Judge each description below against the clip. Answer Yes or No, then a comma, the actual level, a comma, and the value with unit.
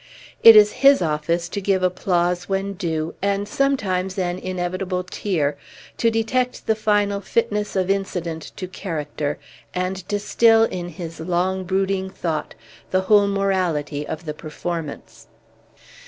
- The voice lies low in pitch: No, medium, 185 Hz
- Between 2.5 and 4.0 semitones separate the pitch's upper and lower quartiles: Yes, average, 2.8 semitones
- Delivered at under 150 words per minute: Yes, slow, 135 wpm